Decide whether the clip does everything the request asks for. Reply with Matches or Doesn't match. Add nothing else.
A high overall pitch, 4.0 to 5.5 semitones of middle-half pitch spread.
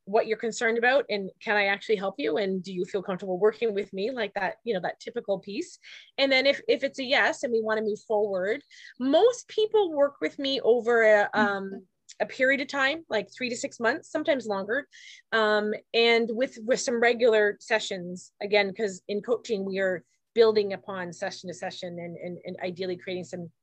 Matches